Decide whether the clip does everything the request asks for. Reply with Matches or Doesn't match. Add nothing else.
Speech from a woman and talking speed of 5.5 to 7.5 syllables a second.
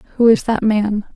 Matches